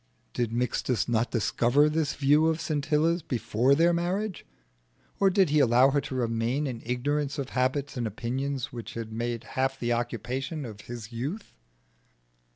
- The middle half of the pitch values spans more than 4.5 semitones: No, average, 3.9 semitones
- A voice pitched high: No, low, 130 Hz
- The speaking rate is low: No, average, 160 wpm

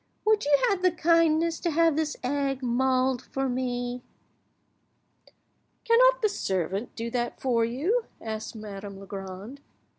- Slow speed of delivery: Yes, slow, 130 wpm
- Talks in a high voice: Yes, very high, 260 Hz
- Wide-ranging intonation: Yes, wide, 6.4 semitones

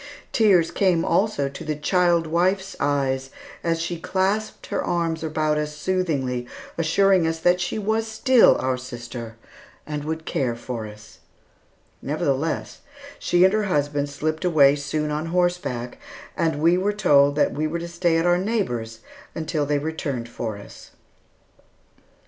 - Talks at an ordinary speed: Yes, average, 150 wpm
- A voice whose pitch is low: No, medium, 160 Hz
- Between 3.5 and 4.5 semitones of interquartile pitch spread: Yes, average, 4.0 semitones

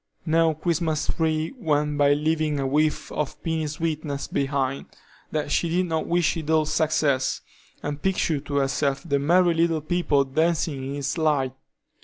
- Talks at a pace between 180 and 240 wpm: No, average, 160 wpm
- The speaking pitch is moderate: Yes, medium, 155 Hz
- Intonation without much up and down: Yes, narrow, 2.3 semitones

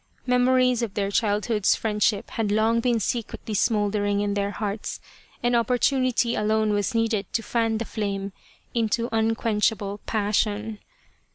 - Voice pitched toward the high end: Yes, high, 220 Hz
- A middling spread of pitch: No, narrow, 2.1 semitones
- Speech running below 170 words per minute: Yes, average, 145 wpm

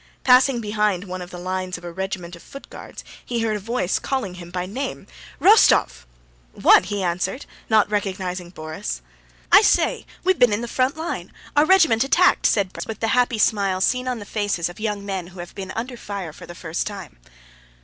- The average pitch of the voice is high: Yes, high, 200 Hz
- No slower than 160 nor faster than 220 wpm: Yes, average, 200 wpm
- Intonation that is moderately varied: Yes, average, 4.5 semitones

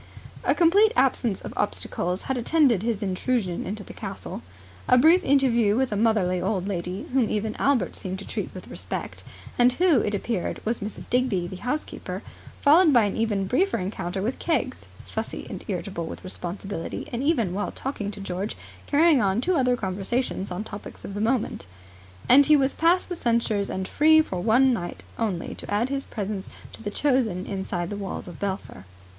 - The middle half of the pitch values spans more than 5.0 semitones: Yes, wide, 5.5 semitones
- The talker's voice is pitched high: Yes, high, 220 Hz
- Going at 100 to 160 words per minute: No, average, 185 wpm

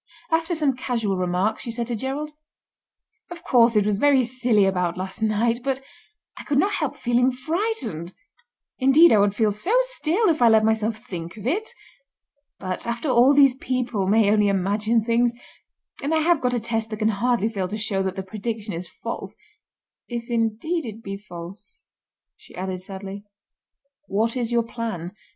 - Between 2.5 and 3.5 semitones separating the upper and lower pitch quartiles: No, average, 4.3 semitones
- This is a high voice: Yes, high, 230 Hz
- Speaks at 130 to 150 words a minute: No, average, 175 wpm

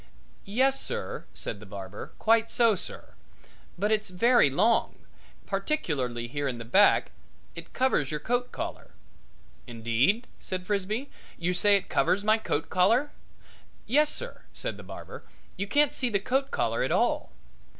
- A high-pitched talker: Yes, high, 200 Hz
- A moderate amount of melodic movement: No, wide, 8.6 semitones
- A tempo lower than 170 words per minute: Yes, average, 150 wpm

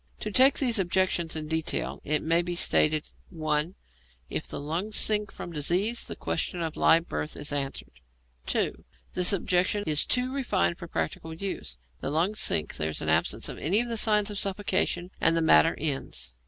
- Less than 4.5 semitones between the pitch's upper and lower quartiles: No, average, 5.0 semitones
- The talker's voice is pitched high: No, medium, 170 Hz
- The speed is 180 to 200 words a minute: Yes, average, 185 wpm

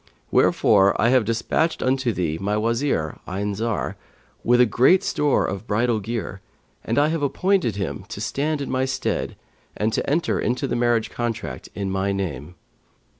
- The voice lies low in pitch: Yes, low, 115 Hz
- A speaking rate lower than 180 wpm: Yes, average, 165 wpm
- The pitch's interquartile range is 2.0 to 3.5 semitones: No, average, 5.0 semitones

